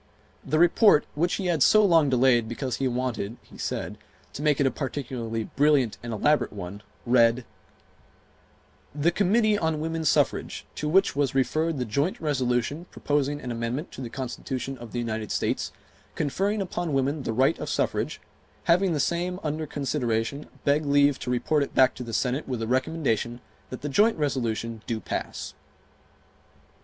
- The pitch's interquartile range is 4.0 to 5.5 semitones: Yes, average, 4.5 semitones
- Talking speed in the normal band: Yes, average, 170 wpm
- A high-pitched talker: No, medium, 140 Hz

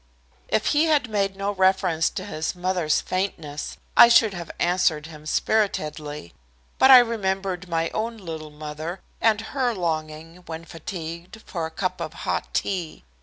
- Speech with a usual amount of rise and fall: Yes, average, 4.2 semitones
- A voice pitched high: No, medium, 180 Hz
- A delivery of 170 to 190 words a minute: No, average, 155 wpm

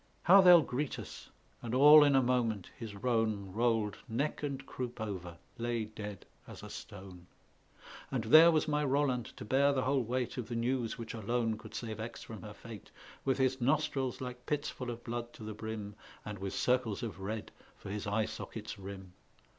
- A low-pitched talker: Yes, low, 120 Hz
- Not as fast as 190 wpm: No, average, 195 wpm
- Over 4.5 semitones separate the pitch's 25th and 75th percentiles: No, average, 3.7 semitones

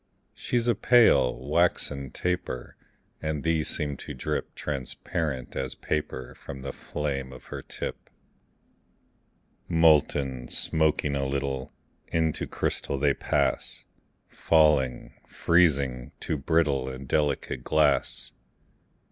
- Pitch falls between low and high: No, very low, 70 Hz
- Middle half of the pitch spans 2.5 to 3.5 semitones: Yes, average, 2.9 semitones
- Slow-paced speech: Yes, slow, 105 wpm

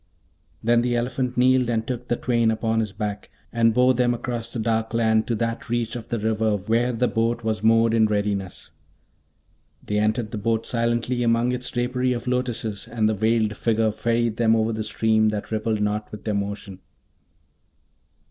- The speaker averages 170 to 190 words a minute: Yes, average, 185 wpm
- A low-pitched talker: Yes, low, 115 Hz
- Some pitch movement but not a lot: No, narrow, 1.6 semitones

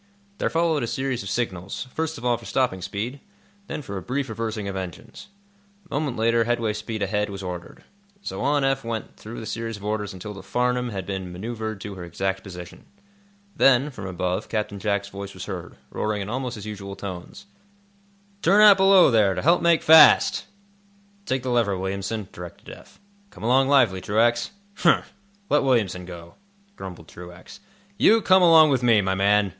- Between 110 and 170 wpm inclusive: No, average, 185 wpm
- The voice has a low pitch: Yes, low, 110 Hz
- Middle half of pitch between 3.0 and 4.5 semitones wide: No, average, 5.1 semitones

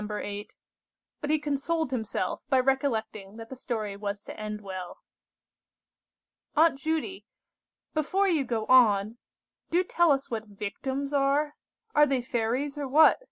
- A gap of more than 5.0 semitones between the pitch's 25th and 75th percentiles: Yes, wide, 5.5 semitones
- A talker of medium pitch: No, very high, 260 Hz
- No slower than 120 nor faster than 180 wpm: Yes, average, 140 wpm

